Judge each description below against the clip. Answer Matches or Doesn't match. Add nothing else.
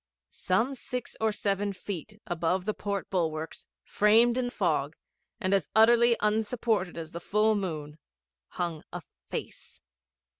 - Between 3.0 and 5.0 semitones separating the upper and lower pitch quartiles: Matches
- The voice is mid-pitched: Doesn't match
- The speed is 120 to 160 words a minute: Matches